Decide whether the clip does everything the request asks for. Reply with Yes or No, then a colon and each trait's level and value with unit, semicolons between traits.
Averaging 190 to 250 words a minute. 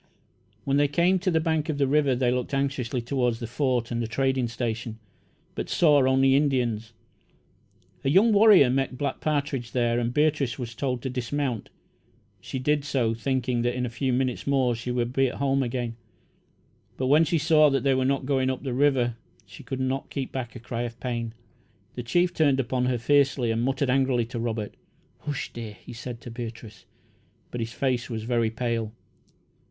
Yes: average, 195 wpm